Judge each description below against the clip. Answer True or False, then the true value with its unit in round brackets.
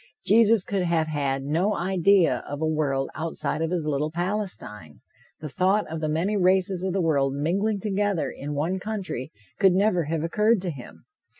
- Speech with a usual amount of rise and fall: True (4.4 semitones)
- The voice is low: False (175 Hz)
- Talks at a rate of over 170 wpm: True (180 wpm)